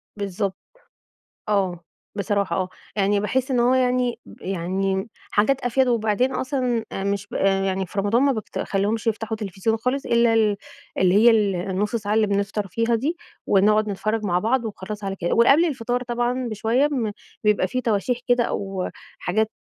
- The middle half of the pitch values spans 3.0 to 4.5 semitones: Yes, average, 3.5 semitones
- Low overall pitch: No, high, 215 Hz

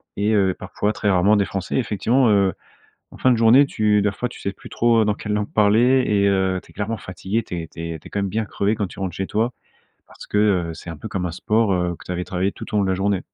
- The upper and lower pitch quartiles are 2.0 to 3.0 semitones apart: Yes, narrow, 2.5 semitones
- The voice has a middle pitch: No, low, 100 Hz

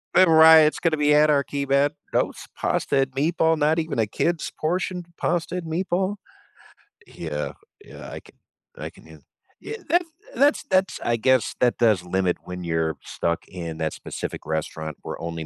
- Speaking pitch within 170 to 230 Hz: No, medium, 145 Hz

